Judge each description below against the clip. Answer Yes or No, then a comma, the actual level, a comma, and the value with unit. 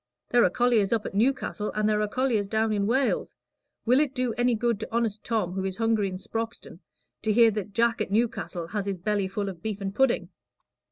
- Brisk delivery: Yes, fast, 220 wpm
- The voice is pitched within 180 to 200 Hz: No, high, 220 Hz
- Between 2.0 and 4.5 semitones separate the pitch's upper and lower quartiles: Yes, average, 2.9 semitones